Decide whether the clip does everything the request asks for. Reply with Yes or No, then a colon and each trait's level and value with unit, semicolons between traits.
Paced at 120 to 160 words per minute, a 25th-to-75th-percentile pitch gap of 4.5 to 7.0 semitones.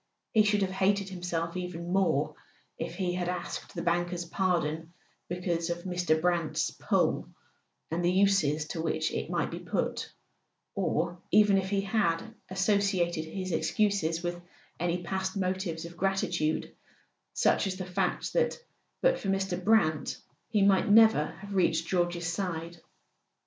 No: average, 150 wpm; narrow, 2.4 semitones